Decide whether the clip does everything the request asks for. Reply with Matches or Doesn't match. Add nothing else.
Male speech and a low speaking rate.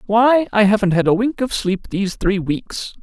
Doesn't match